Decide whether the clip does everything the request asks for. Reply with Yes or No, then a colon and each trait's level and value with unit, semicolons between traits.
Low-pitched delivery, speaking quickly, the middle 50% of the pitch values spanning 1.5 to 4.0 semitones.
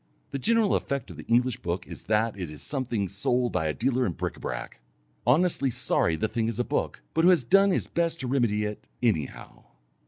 No: low, 120 Hz; fast, 220 wpm; average, 4.8 semitones